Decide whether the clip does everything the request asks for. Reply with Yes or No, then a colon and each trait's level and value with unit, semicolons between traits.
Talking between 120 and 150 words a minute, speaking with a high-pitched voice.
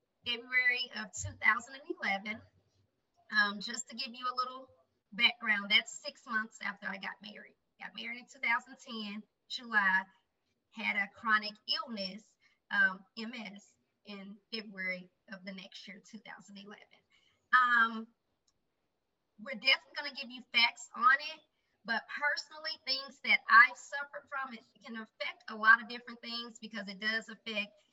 Yes: average, 140 wpm; high, 230 Hz